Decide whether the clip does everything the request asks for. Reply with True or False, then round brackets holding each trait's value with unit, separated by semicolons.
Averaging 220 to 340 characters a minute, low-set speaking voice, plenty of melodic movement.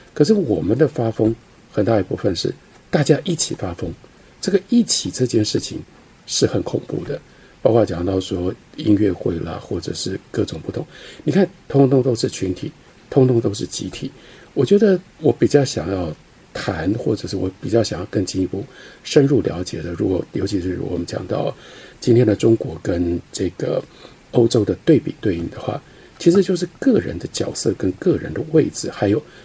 True (265 characters per minute; 115 Hz; 8.3 semitones)